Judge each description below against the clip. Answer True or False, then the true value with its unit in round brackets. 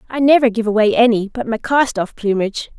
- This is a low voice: False (230 Hz)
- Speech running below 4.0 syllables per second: False (5.9 syllables/s)